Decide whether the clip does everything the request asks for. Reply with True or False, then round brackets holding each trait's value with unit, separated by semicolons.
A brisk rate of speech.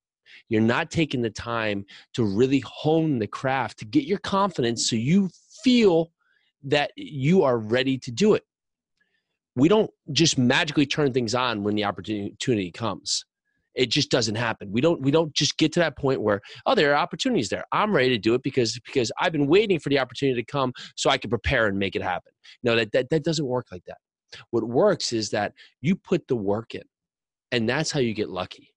True (210 wpm)